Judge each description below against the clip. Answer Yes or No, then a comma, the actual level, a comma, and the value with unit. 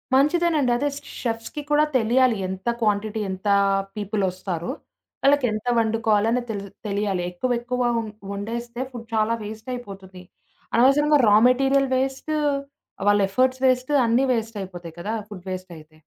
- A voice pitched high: Yes, high, 225 Hz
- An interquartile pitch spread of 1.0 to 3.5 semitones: No, average, 4.2 semitones